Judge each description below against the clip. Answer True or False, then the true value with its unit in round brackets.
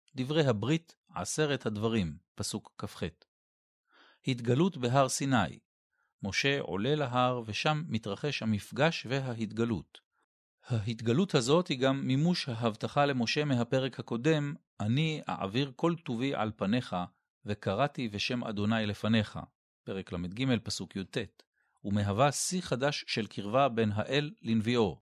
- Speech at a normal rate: True (110 wpm)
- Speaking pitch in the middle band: False (120 Hz)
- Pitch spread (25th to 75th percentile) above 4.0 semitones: True (5.1 semitones)